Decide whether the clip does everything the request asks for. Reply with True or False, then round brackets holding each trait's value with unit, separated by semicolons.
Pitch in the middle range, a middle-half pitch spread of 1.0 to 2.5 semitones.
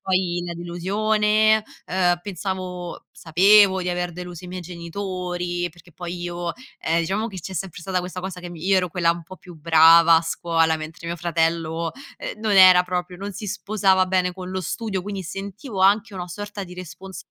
True (180 Hz; 2.0 semitones)